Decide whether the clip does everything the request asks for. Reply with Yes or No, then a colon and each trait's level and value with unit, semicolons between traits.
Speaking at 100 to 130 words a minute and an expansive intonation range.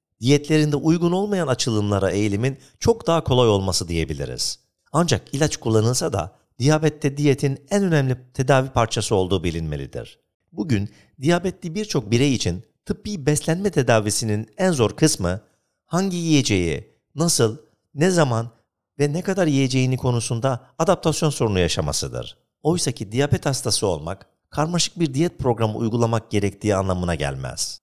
Yes: average, 125 wpm; wide, 6.7 semitones